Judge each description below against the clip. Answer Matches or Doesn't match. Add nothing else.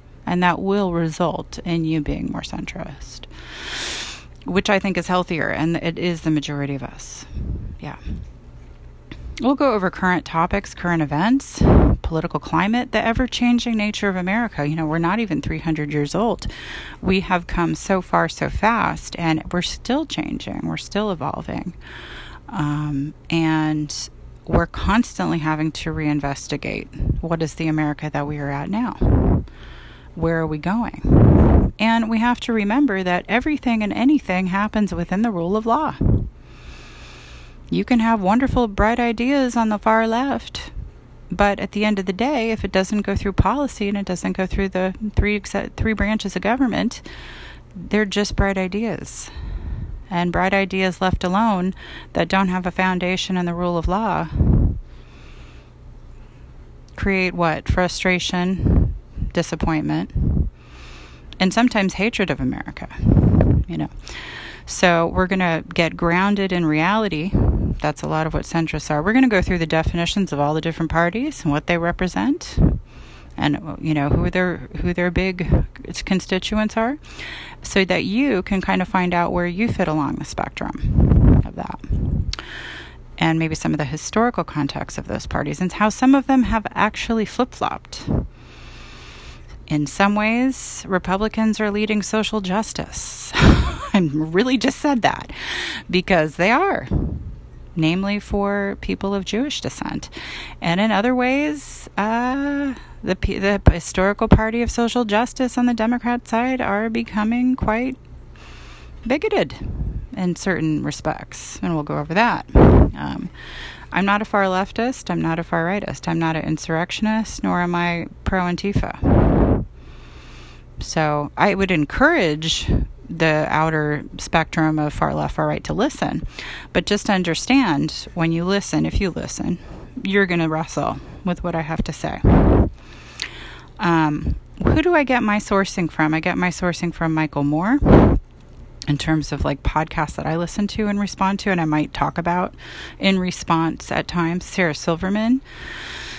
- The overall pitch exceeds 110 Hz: Matches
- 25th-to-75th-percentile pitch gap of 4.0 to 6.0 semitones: Matches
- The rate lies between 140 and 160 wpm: Matches